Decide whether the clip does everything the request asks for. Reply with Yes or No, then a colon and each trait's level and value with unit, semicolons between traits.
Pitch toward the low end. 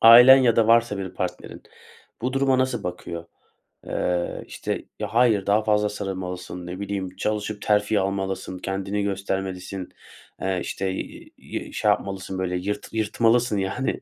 Yes: low, 100 Hz